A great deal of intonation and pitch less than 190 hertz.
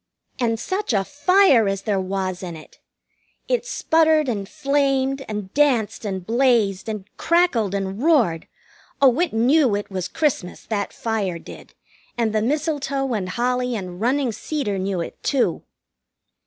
No: wide, 6.1 semitones; high, 230 Hz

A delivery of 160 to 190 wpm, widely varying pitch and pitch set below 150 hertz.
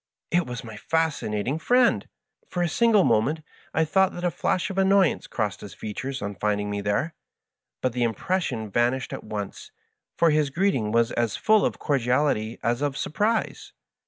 Yes: average, 175 wpm; wide, 8.1 semitones; low, 135 Hz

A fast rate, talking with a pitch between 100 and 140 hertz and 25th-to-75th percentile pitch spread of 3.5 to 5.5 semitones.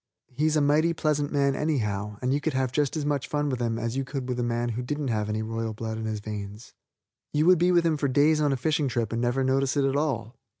Yes: fast, 275 wpm; low, 135 Hz; average, 4.3 semitones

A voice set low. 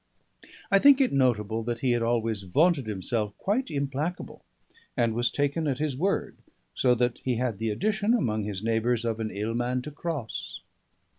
Yes: low, 125 Hz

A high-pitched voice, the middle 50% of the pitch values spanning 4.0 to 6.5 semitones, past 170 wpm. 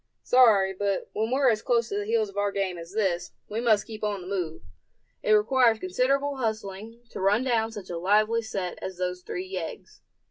No: high, 210 Hz; average, 3.2 semitones; fast, 205 wpm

